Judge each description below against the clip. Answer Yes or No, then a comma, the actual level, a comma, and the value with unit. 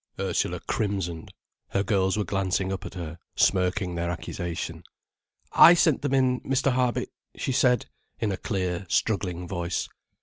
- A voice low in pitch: Yes, very low, 95 Hz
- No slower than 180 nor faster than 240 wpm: No, average, 145 wpm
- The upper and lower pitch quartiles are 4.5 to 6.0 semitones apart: Yes, average, 5.0 semitones